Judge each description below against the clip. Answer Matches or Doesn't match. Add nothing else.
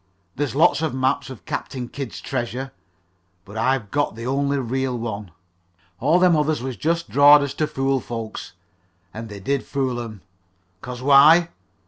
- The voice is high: Doesn't match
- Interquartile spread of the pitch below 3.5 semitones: Matches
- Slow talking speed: Doesn't match